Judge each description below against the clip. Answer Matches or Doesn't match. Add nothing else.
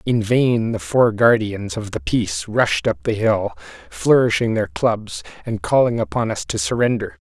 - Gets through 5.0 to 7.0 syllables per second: Doesn't match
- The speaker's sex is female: Doesn't match